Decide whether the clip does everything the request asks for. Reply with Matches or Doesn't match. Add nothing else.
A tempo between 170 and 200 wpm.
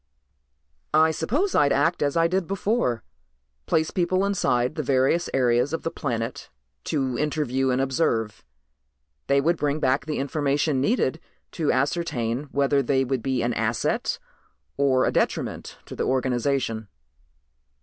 Doesn't match